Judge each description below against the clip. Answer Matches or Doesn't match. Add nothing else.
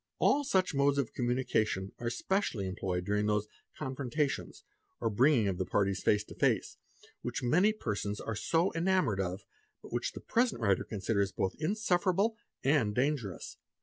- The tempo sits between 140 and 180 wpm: Matches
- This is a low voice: Matches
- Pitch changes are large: Matches